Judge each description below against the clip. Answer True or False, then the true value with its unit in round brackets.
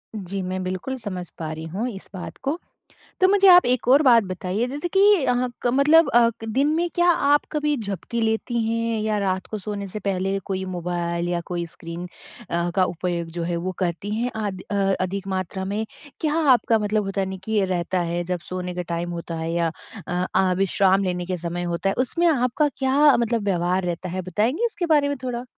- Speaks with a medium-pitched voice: False (195 Hz)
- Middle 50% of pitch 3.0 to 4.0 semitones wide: False (5.2 semitones)